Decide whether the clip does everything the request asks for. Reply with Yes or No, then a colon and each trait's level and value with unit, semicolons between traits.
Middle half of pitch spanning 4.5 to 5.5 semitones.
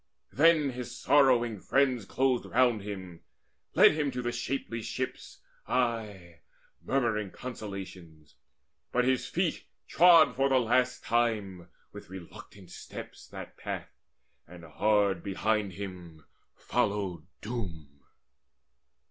Yes: average, 5.1 semitones